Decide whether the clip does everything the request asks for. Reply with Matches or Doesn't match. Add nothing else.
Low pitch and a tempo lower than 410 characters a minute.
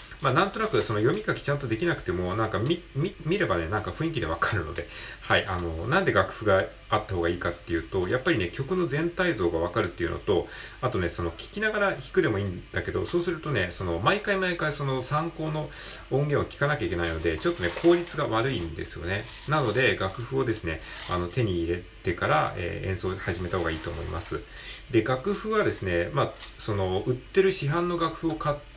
Doesn't match